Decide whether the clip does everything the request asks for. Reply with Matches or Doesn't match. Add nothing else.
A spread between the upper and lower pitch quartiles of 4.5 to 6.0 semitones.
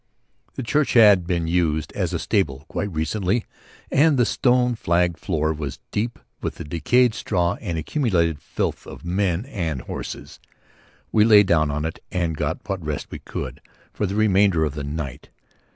Matches